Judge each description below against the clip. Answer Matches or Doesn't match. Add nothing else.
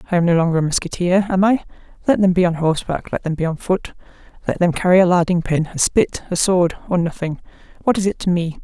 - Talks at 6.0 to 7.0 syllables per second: Matches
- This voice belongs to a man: Doesn't match